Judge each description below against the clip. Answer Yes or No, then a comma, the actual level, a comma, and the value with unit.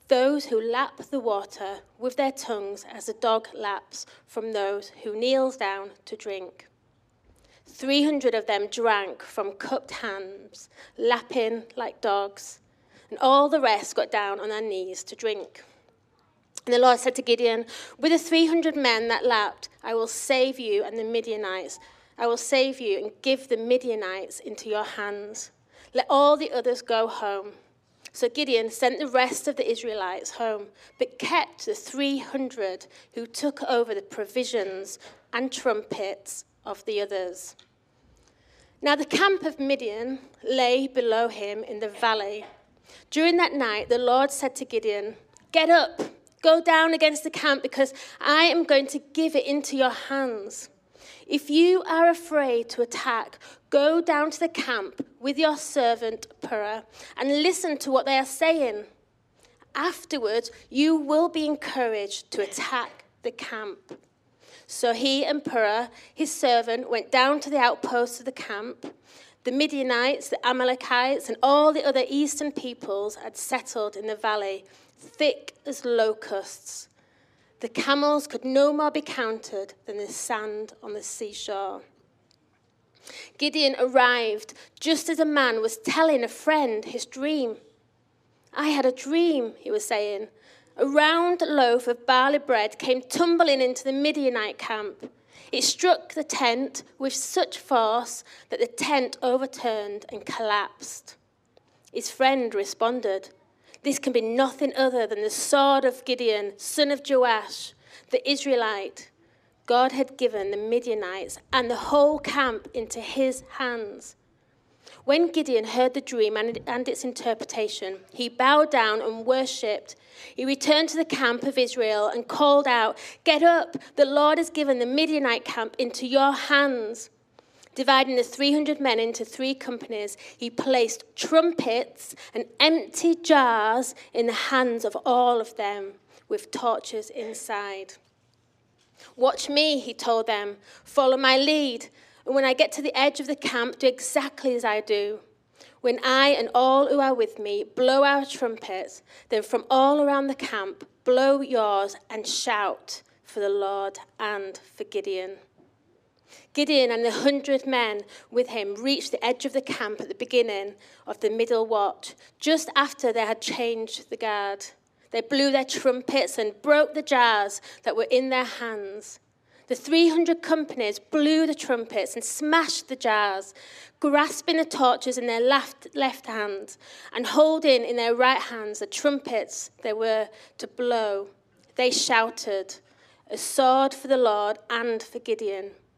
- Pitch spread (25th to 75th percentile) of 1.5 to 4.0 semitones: No, average, 4.6 semitones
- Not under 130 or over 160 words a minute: Yes, average, 155 wpm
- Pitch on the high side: Yes, very high, 255 Hz